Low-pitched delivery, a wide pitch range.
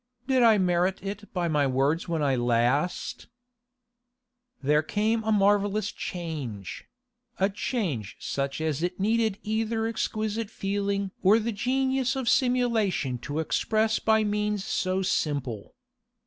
No: high, 200 Hz; wide, 5.9 semitones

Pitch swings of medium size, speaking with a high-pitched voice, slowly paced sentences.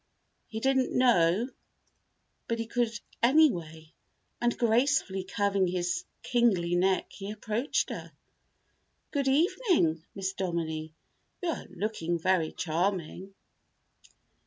No: wide, 5.7 semitones; high, 195 Hz; slow, 105 wpm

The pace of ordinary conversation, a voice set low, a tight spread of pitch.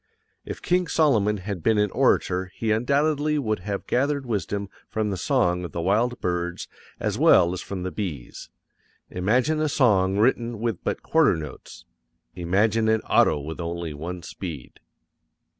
No: average, 160 wpm; low, 105 Hz; average, 5.2 semitones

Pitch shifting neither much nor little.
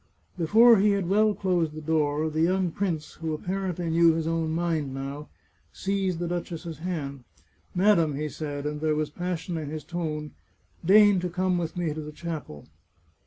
Yes: average, 3.0 semitones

